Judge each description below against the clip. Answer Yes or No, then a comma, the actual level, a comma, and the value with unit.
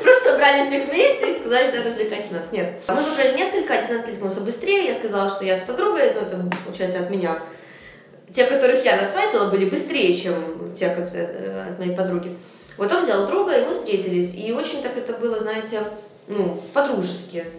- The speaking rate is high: Yes, fast, 185 wpm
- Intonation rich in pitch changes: Yes, wide, 7.5 semitones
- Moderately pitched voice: No, high, 215 Hz